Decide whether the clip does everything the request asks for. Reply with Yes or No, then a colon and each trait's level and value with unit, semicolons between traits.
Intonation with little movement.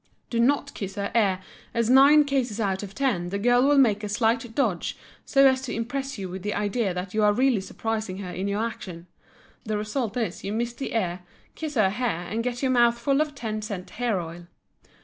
No: average, 4.1 semitones